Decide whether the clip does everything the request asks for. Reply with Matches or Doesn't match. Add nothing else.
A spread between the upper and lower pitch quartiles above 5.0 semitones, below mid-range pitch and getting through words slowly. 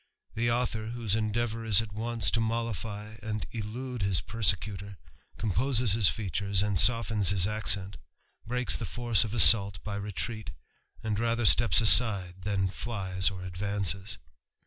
Doesn't match